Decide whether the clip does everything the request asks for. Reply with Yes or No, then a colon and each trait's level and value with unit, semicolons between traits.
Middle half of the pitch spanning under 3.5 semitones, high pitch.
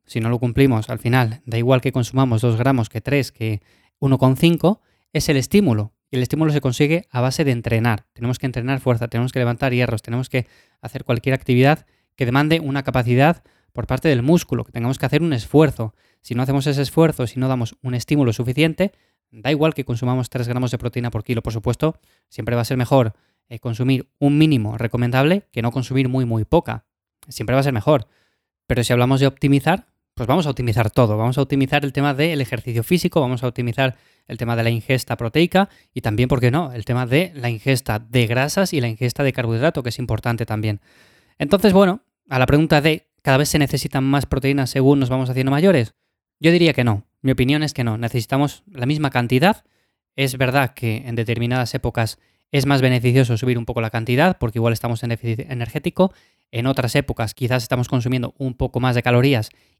No: average, 2.9 semitones; low, 130 Hz